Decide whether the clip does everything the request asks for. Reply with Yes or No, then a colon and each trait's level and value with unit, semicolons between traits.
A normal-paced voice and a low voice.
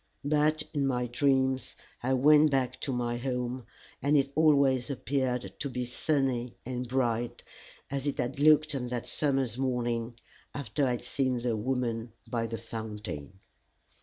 Yes: average, 155 wpm; low, 130 Hz